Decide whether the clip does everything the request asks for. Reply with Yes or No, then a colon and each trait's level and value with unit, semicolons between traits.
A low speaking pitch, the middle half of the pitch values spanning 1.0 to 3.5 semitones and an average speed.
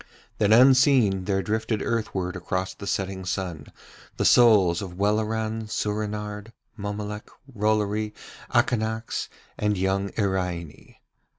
No: low, 105 Hz; narrow, 2.4 semitones; slow, 105 wpm